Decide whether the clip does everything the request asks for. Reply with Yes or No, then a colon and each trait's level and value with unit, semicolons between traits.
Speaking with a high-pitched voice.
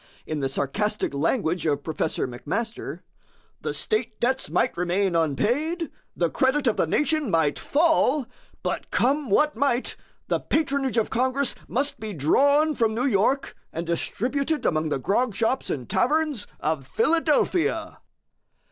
Yes: high, 235 Hz